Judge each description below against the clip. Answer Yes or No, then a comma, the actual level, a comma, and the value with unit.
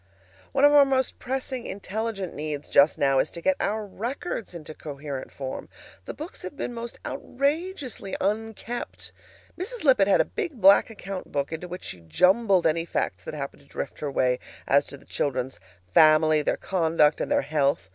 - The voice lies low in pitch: No, medium, 185 Hz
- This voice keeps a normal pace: Yes, average, 180 wpm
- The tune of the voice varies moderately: No, wide, 8.5 semitones